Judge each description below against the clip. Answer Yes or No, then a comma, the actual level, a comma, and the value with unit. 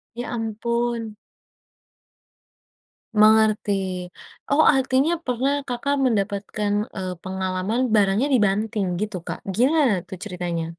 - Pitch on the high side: Yes, high, 220 Hz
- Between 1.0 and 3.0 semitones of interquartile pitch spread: No, average, 3.7 semitones